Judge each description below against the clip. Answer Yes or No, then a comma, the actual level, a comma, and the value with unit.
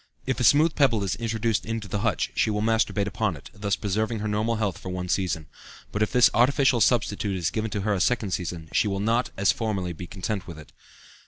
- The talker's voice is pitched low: Yes, low, 105 Hz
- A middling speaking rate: No, fast, 230 wpm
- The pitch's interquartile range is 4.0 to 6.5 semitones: No, average, 3.1 semitones